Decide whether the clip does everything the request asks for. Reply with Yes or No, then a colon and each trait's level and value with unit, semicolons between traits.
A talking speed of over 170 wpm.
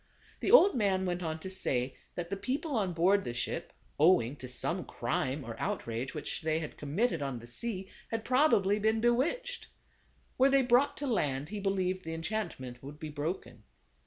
Yes: average, 190 wpm